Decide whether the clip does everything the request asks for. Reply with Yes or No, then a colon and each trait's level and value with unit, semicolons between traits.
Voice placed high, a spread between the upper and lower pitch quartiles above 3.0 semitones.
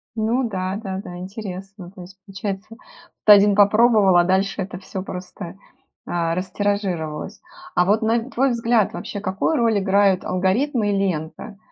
No: high, 195 Hz; average, 2.7 semitones